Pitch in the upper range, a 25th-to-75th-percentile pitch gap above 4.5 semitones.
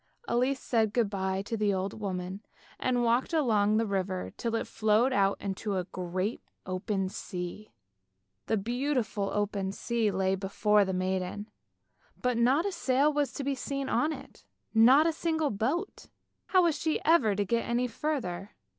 Yes: high, 220 Hz; average, 5.0 semitones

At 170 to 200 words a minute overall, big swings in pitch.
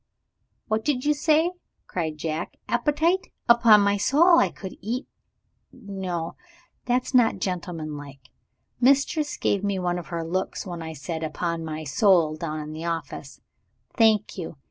No: average, 150 wpm; wide, 6.9 semitones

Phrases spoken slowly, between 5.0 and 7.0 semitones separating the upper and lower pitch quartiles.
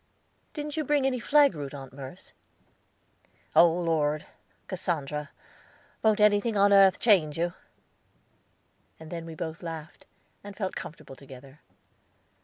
Yes: slow, 125 wpm; wide, 5.5 semitones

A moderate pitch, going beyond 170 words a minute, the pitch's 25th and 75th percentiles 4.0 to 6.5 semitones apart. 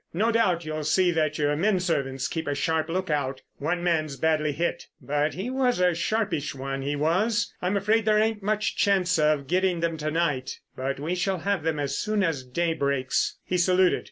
Yes: medium, 165 Hz; average, 200 wpm; average, 4.3 semitones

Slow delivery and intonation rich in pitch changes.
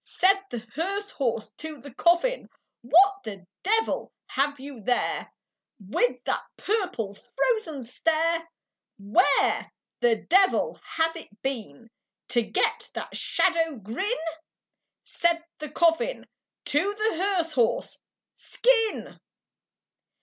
Yes: slow, 110 wpm; wide, 7.8 semitones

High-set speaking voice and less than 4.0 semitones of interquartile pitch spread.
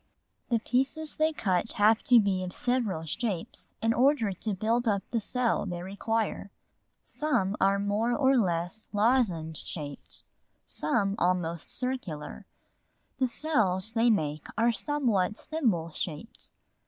No: high, 215 Hz; average, 5.0 semitones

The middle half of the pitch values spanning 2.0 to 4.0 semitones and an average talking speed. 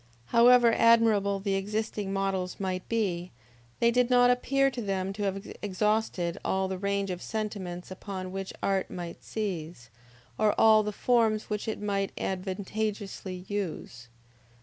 Yes: average, 2.7 semitones; average, 145 wpm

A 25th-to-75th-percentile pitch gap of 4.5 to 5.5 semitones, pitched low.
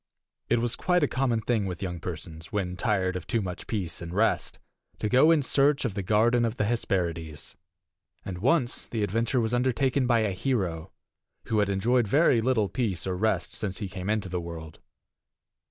Yes: average, 4.9 semitones; low, 105 Hz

